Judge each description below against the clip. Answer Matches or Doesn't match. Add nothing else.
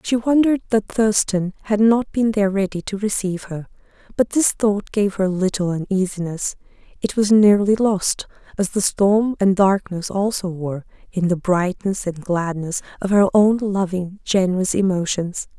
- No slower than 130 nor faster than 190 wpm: Matches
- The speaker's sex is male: Doesn't match